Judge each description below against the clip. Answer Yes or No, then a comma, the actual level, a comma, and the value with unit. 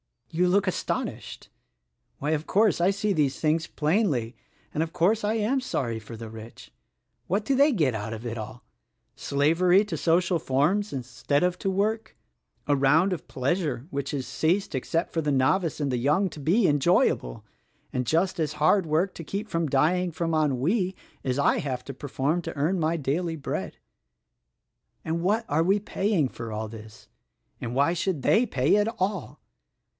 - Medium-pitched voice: Yes, medium, 160 Hz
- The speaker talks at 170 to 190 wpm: Yes, average, 180 wpm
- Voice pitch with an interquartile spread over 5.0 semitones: Yes, wide, 5.6 semitones